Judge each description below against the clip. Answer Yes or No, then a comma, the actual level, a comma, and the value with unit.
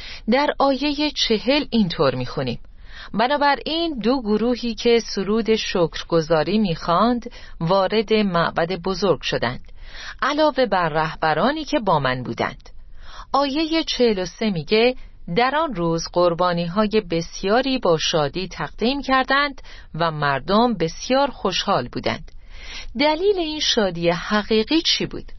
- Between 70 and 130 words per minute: Yes, average, 115 wpm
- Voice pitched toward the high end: Yes, high, 220 Hz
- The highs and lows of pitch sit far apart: Yes, wide, 7.5 semitones